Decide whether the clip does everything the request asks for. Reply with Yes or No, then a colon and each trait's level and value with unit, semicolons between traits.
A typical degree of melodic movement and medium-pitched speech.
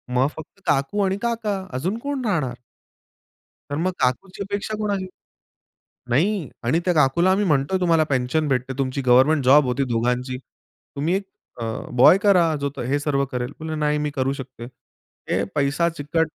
No: wide, 6.0 semitones; medium, 150 Hz